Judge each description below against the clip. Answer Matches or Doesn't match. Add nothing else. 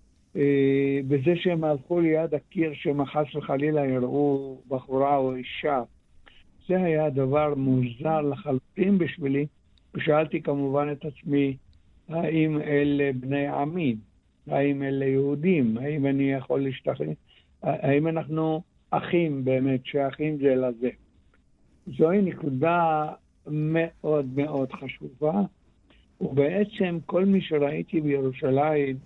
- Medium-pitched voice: Matches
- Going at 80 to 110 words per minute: Matches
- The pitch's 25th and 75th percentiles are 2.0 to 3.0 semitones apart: Matches